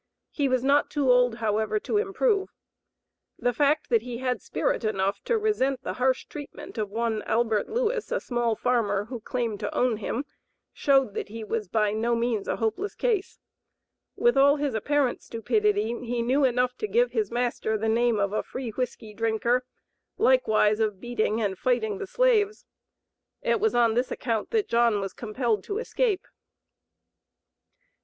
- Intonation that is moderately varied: Yes, average, 4.6 semitones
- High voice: Yes, high, 240 Hz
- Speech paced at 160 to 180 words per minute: Yes, average, 170 wpm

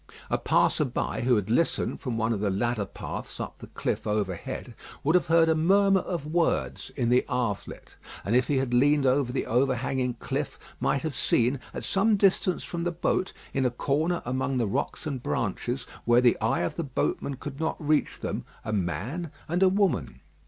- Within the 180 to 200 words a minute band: Yes, average, 195 wpm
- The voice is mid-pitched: No, low, 130 Hz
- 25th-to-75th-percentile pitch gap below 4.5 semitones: No, average, 5.3 semitones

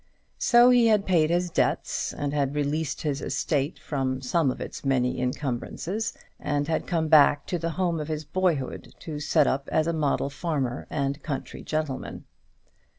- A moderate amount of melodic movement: Yes, average, 3.3 semitones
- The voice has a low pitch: No, medium, 150 Hz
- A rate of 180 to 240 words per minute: No, average, 170 wpm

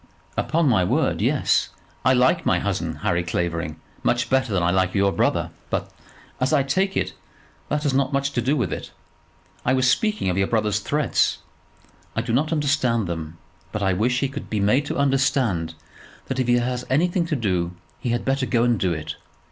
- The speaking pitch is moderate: No, low, 120 Hz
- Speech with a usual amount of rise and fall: No, wide, 6.5 semitones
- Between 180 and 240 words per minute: Yes, average, 200 wpm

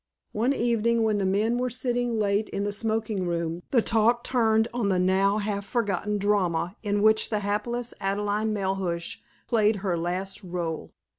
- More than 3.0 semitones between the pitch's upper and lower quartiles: No, average, 2.7 semitones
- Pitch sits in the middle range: No, high, 210 Hz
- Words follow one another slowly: No, average, 165 wpm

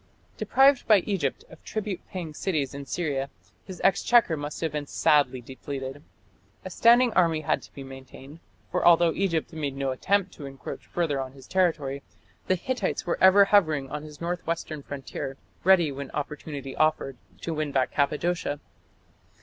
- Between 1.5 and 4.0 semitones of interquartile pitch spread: No, average, 4.6 semitones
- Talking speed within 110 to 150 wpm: No, average, 165 wpm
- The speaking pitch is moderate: Yes, medium, 155 Hz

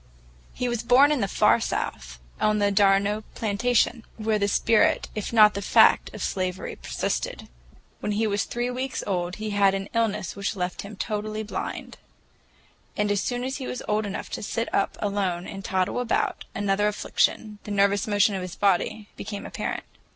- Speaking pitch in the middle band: No, high, 205 Hz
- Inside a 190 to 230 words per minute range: No, average, 180 wpm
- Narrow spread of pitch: Yes, narrow, 1.9 semitones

